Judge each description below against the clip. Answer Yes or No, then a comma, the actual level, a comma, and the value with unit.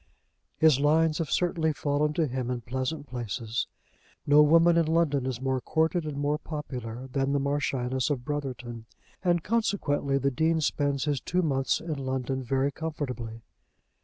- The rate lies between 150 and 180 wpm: Yes, average, 160 wpm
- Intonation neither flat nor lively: Yes, average, 3.4 semitones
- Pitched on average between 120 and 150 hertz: Yes, medium, 140 Hz